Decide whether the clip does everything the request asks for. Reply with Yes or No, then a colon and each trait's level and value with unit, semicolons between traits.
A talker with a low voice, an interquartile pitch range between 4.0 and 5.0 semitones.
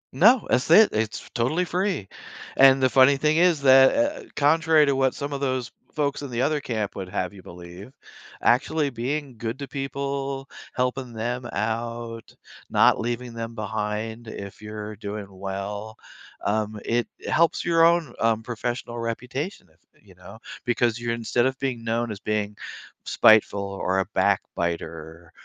Yes: low, 120 Hz; average, 4.4 semitones